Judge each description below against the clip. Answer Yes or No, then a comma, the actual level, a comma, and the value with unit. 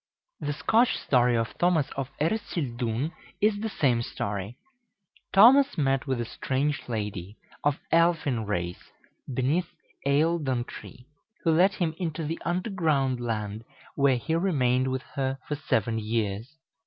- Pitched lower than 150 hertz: Yes, low, 135 Hz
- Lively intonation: Yes, wide, 5.7 semitones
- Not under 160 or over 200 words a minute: No, slow, 135 wpm